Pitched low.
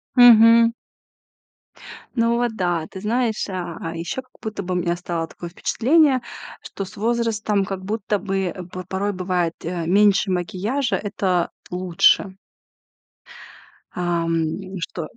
No: high, 190 Hz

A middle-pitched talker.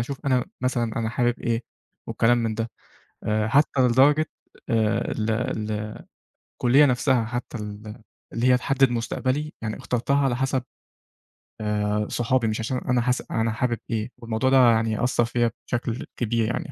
No: low, 120 Hz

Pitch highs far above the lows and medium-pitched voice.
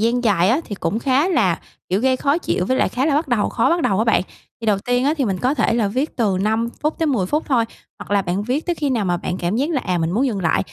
No: wide, 5.7 semitones; high, 235 Hz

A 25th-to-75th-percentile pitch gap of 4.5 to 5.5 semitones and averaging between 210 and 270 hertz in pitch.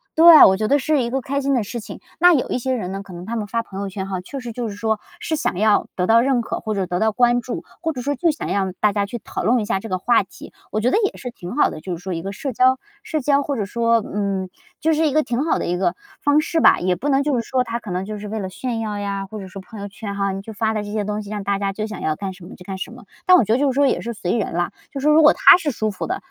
Yes: average, 4.8 semitones; high, 220 Hz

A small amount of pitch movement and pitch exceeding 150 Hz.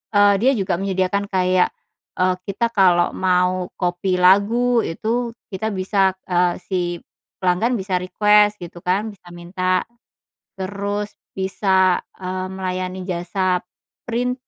Yes: narrow, 1.9 semitones; high, 190 Hz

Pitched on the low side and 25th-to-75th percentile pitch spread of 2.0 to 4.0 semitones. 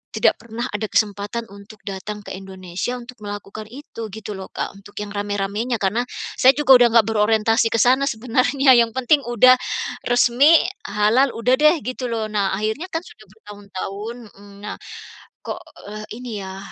No: high, 220 Hz; average, 3.2 semitones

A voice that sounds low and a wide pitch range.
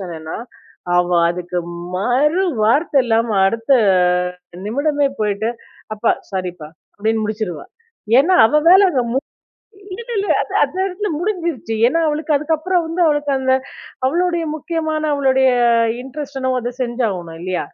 No: very high, 265 Hz; wide, 6.7 semitones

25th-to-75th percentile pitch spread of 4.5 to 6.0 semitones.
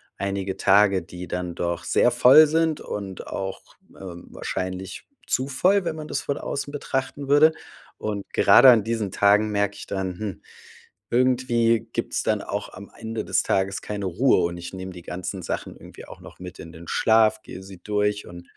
Yes: average, 5.1 semitones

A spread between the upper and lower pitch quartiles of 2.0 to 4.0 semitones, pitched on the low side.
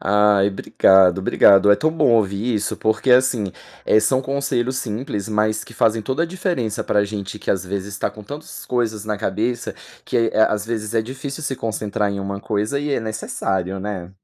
Yes: average, 3.6 semitones; low, 110 Hz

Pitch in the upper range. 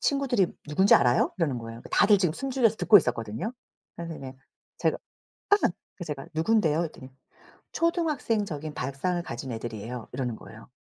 No: medium, 155 Hz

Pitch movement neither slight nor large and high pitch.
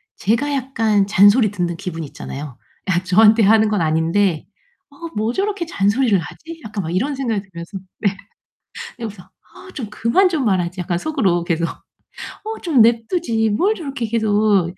No: wide, 6.0 semitones; high, 215 Hz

